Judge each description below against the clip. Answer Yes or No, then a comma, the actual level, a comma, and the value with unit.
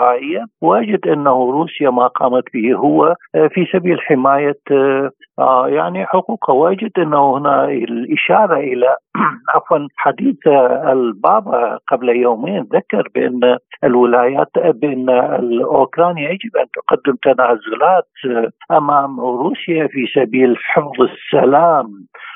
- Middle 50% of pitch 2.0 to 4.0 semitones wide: No, average, 5.3 semitones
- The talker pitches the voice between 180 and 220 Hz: No, medium, 140 Hz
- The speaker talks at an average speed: Yes, average, 100 wpm